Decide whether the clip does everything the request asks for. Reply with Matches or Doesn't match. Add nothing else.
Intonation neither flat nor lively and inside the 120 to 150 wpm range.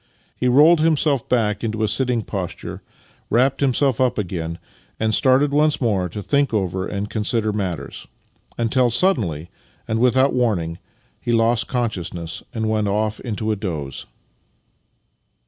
Matches